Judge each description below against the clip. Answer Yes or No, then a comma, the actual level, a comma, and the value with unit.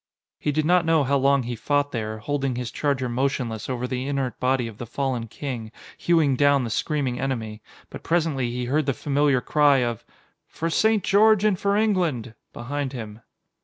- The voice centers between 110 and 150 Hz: Yes, low, 135 Hz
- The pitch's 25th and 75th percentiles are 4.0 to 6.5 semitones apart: No, average, 3.6 semitones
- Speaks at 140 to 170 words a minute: No, average, 185 wpm